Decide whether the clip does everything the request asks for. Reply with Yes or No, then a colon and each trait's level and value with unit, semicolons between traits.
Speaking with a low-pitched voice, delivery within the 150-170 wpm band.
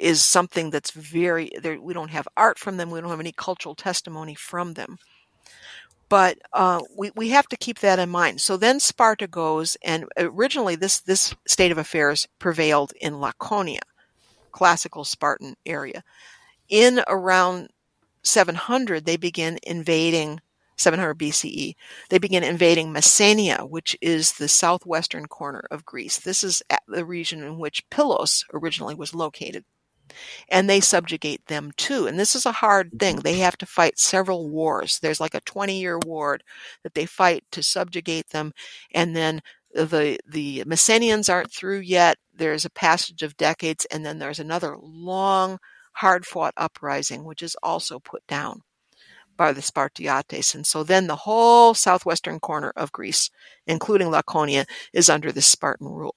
No: medium, 170 Hz; average, 160 wpm